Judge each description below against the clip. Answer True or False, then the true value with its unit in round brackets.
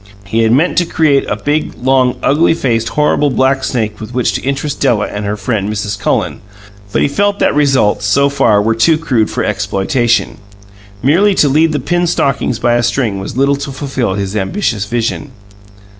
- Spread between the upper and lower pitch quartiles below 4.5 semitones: False (5.0 semitones)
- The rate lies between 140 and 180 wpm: False (190 wpm)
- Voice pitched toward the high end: False (125 Hz)